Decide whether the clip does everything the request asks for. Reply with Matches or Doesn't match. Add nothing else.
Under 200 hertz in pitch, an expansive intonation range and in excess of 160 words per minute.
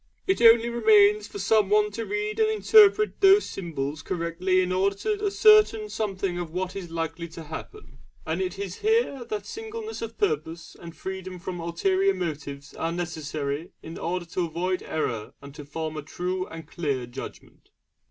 Matches